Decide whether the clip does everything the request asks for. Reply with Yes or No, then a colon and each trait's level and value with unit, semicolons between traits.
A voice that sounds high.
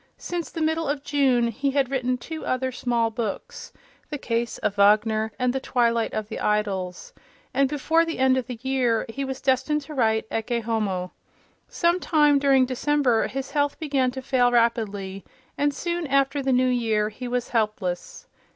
Yes: very high, 250 Hz